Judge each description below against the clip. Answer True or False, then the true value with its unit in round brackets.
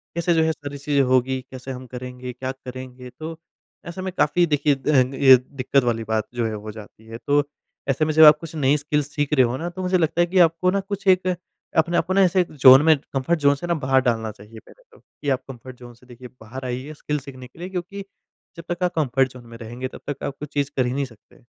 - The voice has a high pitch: False (140 Hz)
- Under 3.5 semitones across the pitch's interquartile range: False (4.2 semitones)